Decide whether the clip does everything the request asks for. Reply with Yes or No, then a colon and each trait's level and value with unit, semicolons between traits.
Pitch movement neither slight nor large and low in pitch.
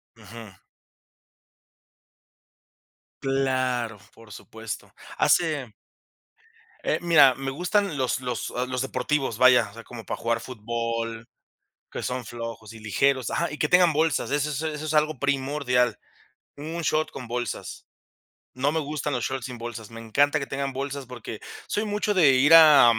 Yes: average, 4.2 semitones; low, 130 Hz